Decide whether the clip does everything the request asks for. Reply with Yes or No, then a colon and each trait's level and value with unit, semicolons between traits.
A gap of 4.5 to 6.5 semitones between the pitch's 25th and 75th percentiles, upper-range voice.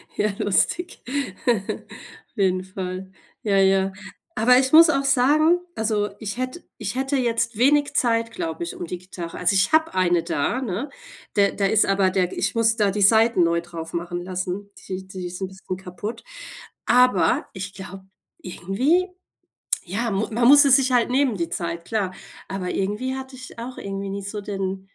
Yes: average, 4.9 semitones; high, 200 Hz